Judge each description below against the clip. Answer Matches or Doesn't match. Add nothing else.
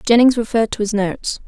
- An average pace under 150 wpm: Doesn't match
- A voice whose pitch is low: Doesn't match